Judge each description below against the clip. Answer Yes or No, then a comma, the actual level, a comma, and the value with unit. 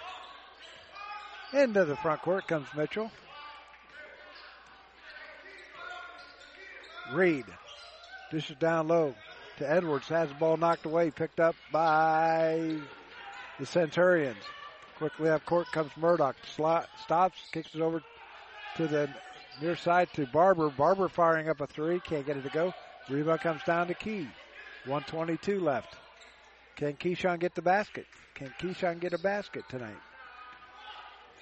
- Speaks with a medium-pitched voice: Yes, medium, 170 Hz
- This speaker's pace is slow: Yes, slow, 125 wpm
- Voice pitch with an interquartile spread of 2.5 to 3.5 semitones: No, average, 5.0 semitones